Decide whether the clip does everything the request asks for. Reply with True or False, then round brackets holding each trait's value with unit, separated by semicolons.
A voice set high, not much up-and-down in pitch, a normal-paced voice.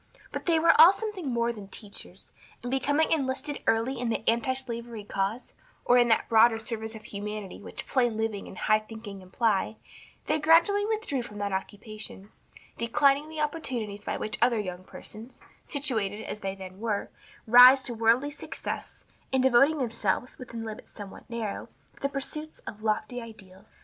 False (230 Hz; 3.9 semitones; 165 wpm)